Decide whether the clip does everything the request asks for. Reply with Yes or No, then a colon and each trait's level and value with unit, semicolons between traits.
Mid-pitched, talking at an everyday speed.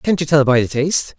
No: medium, 145 Hz; fast, 305 wpm